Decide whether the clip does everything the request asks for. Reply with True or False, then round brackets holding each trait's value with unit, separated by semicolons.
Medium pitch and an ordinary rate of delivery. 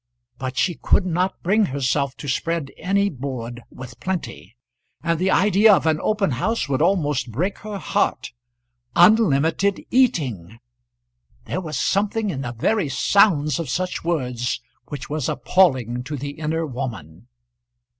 True (155 Hz; 145 wpm)